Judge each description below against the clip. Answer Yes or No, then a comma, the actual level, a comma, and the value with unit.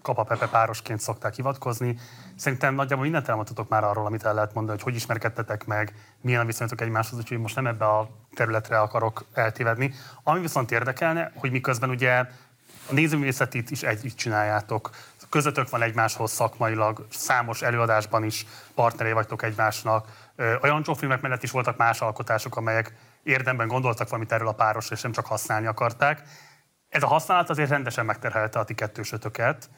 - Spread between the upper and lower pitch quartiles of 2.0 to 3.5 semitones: Yes, average, 2.9 semitones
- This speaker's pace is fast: Yes, fast, 160 wpm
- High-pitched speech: No, low, 115 Hz